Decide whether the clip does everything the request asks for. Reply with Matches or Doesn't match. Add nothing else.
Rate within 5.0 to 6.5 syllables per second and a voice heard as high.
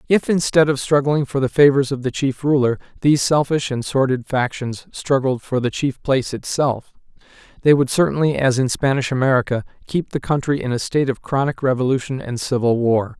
Doesn't match